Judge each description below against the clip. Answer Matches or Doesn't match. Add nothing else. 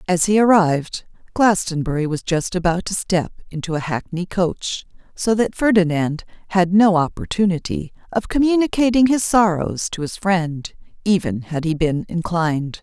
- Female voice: Matches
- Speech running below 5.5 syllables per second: Matches